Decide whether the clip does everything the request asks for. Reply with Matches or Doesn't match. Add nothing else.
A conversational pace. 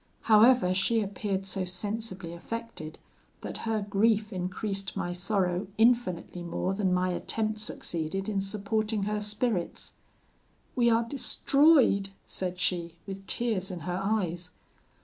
Doesn't match